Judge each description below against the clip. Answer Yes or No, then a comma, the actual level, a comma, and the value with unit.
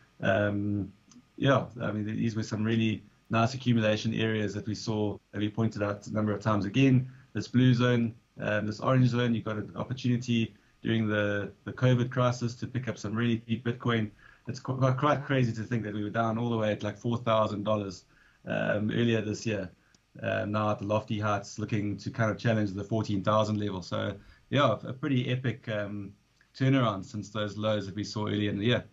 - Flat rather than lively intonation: Yes, narrow, 2.3 semitones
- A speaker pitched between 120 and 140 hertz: No, low, 110 Hz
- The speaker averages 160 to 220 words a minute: Yes, average, 200 wpm